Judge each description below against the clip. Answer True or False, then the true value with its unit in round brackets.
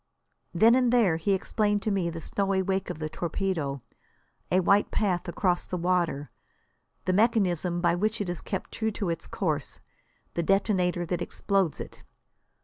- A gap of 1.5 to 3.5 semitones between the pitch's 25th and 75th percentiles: True (2.7 semitones)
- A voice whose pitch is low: False (185 Hz)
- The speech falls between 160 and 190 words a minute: True (165 wpm)